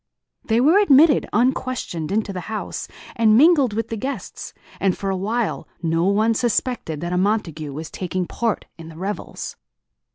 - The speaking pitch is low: No, high, 210 Hz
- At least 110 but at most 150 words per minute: No, average, 160 wpm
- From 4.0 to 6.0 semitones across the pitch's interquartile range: Yes, average, 5.1 semitones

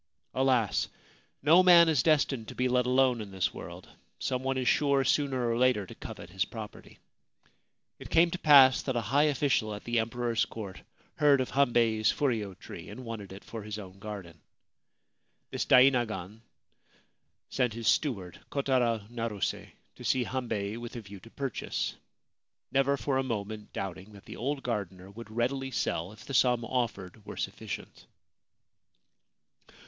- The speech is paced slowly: No, average, 160 wpm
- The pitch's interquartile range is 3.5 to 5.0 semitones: Yes, average, 4.1 semitones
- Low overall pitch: Yes, low, 120 Hz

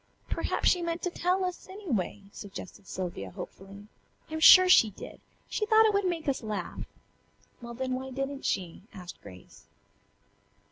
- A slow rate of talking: No, average, 155 wpm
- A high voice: Yes, very high, 260 Hz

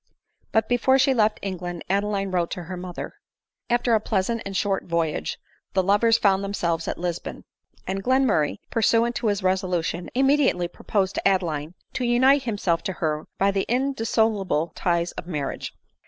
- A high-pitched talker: Yes, high, 195 Hz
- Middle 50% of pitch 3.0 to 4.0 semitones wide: No, average, 4.5 semitones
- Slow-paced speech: No, average, 160 wpm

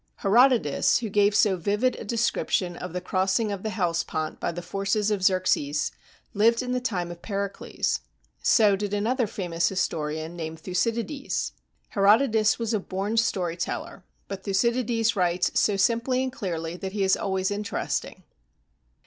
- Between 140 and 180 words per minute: Yes, average, 155 wpm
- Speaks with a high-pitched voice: Yes, high, 200 Hz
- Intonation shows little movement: No, average, 3.9 semitones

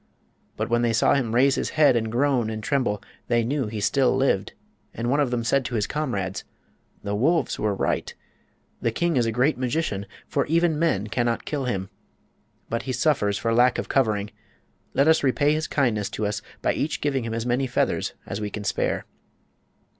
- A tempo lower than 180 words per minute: No, average, 200 wpm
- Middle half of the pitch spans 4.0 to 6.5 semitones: Yes, average, 4.4 semitones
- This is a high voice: No, low, 120 Hz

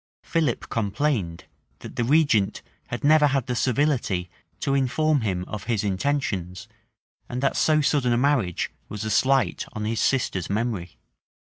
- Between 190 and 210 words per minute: No, average, 155 wpm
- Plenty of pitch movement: Yes, wide, 6.0 semitones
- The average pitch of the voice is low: Yes, low, 120 Hz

